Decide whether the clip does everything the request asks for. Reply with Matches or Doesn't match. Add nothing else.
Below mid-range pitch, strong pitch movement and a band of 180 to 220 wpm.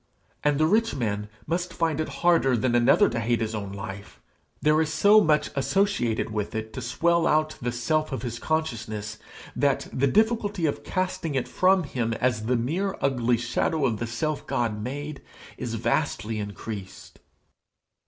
Doesn't match